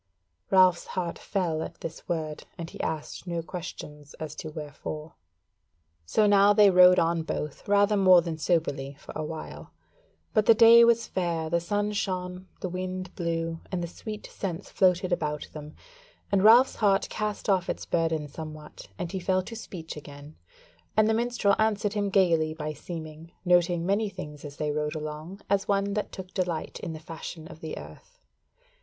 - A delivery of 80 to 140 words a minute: No, average, 175 wpm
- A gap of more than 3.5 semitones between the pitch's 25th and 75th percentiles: Yes, average, 3.9 semitones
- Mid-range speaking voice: Yes, medium, 175 Hz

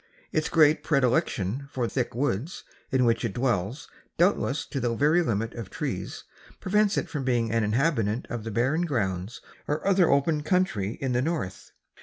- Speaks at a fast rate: No, average, 170 wpm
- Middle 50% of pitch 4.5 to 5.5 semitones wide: Yes, average, 5.2 semitones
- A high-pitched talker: No, low, 130 Hz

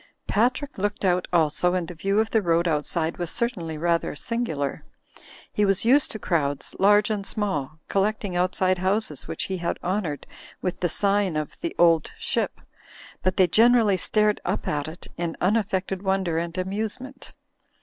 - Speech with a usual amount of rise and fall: Yes, average, 3.7 semitones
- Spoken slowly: No, average, 165 wpm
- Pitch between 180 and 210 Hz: Yes, medium, 185 Hz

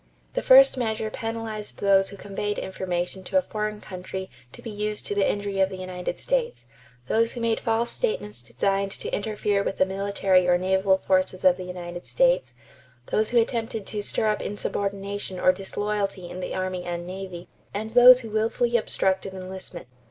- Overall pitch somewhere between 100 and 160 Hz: No, high, 200 Hz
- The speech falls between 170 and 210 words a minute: Yes, average, 180 wpm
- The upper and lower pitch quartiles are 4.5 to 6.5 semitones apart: No, average, 2.8 semitones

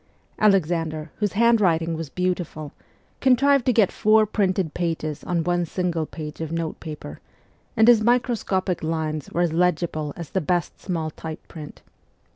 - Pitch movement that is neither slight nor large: Yes, average, 4.2 semitones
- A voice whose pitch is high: No, medium, 175 Hz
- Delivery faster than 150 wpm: No, average, 145 wpm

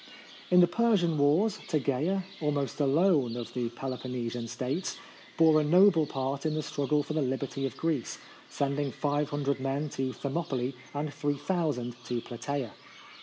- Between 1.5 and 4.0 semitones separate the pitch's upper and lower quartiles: Yes, average, 3.1 semitones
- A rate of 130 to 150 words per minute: Yes, average, 145 wpm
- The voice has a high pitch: No, medium, 145 Hz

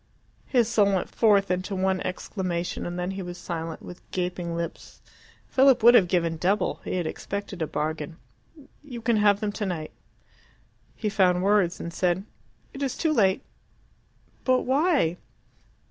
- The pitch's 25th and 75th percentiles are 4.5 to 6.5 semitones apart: No, average, 3.5 semitones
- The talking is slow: No, average, 155 wpm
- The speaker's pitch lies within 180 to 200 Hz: Yes, high, 190 Hz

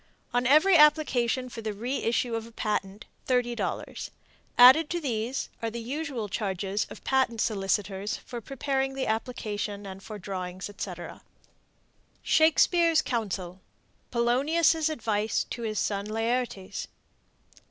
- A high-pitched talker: Yes, high, 230 Hz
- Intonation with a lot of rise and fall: No, average, 4.5 semitones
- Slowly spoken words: Yes, slow, 120 wpm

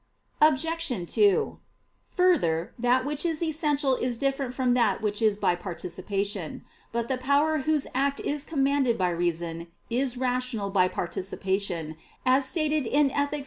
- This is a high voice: Yes, very high, 255 Hz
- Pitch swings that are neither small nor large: No, wide, 6.4 semitones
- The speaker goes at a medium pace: Yes, average, 145 wpm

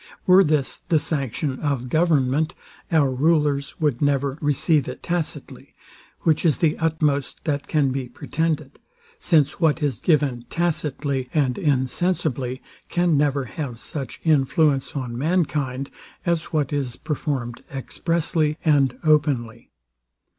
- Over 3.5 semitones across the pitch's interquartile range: No, average, 3.0 semitones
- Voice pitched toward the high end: No, medium, 145 Hz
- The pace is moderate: No, slow, 125 wpm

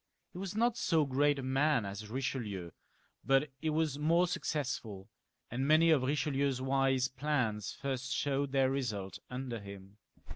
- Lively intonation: No, average, 3.6 semitones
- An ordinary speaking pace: Yes, average, 155 wpm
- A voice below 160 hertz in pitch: Yes, low, 135 Hz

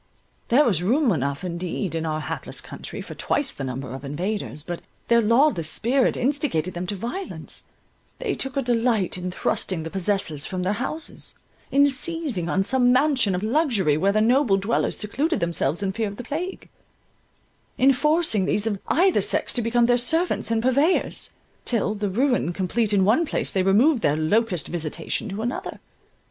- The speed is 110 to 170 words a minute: No, average, 180 wpm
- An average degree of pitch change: No, wide, 6.4 semitones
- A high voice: Yes, high, 215 Hz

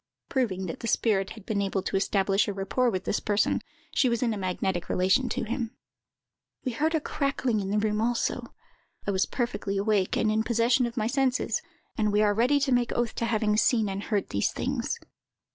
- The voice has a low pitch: No, high, 215 Hz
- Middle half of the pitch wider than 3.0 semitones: Yes, average, 3.4 semitones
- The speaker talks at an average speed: No, fast, 210 wpm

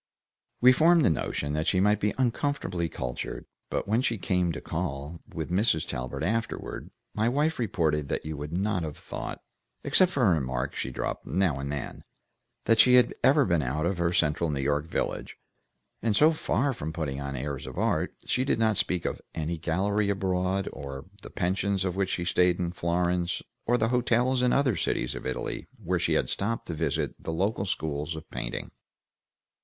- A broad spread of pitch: Yes, wide, 6.1 semitones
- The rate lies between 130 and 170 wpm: No, average, 195 wpm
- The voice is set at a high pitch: No, very low, 90 Hz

